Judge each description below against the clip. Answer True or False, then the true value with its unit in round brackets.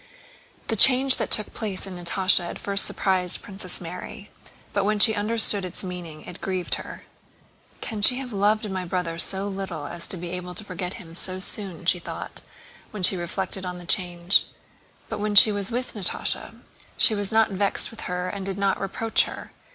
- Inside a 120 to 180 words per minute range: False (190 wpm)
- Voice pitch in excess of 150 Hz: True (190 Hz)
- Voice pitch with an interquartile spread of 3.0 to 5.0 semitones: False (2.5 semitones)